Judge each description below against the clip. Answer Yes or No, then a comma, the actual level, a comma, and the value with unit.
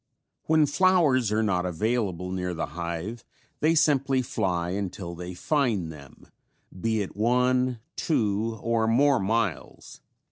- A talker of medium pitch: No, low, 110 Hz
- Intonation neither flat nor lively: No, wide, 5.9 semitones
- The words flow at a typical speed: No, slow, 130 wpm